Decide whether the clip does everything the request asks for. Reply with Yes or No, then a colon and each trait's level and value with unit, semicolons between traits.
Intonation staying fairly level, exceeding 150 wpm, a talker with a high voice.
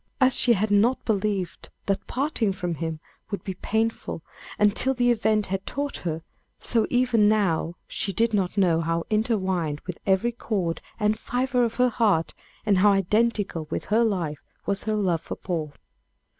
No: average, 4.1 semitones; average, 170 wpm; high, 205 Hz